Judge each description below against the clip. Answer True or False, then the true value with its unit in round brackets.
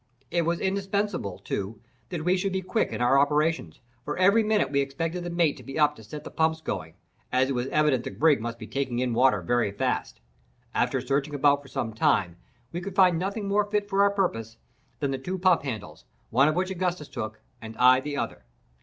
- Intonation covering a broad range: True (6.6 semitones)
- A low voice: False (150 Hz)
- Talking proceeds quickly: True (220 wpm)